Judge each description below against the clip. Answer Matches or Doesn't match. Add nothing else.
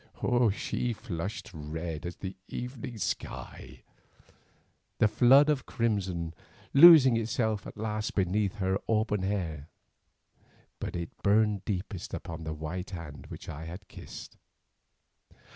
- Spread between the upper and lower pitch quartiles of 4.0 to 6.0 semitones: Matches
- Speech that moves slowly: Matches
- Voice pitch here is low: Matches